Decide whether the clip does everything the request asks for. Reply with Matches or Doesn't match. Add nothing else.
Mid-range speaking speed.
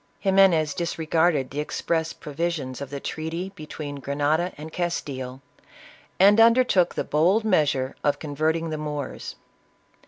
Doesn't match